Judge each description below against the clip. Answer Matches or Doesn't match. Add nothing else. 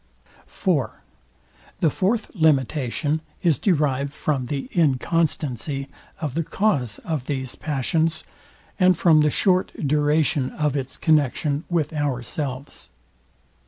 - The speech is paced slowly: Matches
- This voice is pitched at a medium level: Matches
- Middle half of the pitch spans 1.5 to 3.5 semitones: Matches